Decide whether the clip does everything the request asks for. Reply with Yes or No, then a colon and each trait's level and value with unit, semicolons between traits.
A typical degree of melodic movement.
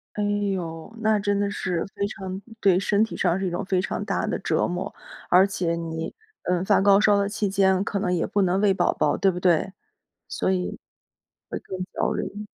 No: narrow, 2.0 semitones